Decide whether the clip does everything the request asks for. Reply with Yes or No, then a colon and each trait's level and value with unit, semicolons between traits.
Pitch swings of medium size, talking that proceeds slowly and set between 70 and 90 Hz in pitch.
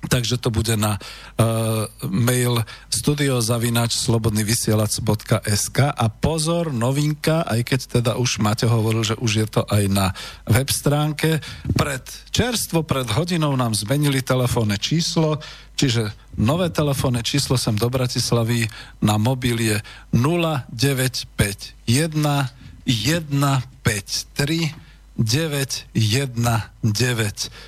No: average, 3.9 semitones; slow, 100 wpm; low, 125 Hz